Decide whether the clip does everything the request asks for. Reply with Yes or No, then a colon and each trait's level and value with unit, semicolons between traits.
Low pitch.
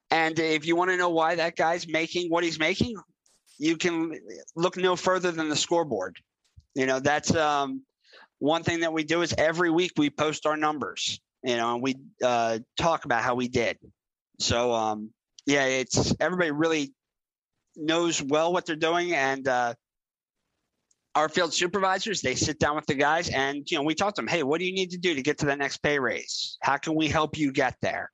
No: medium, 155 Hz